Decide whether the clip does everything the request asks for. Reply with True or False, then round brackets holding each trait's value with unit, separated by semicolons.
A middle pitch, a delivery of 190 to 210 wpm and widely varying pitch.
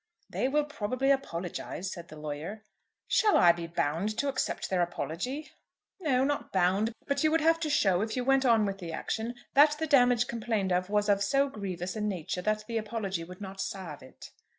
False (215 Hz; 200 wpm; 6.6 semitones)